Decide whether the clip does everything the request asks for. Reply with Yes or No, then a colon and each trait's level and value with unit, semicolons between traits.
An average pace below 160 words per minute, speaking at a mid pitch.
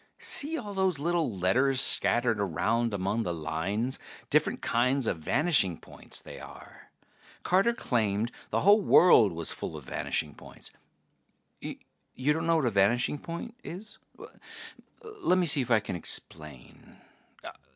No: average, 140 wpm; low, 125 Hz